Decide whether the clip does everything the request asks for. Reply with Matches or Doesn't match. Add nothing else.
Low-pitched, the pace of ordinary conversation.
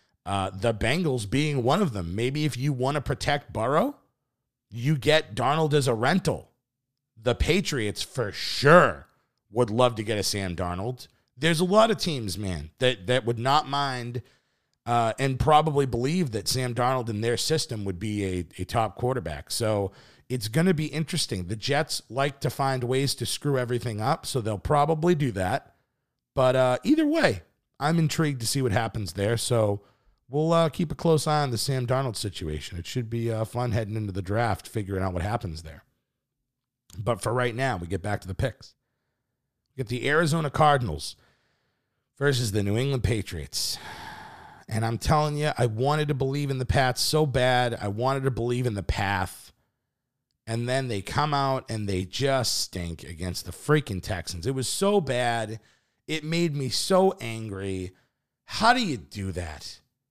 Matches